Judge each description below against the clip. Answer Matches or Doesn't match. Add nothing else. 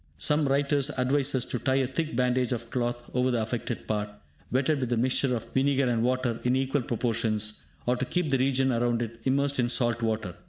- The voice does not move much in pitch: Matches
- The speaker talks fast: Matches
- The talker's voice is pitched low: Matches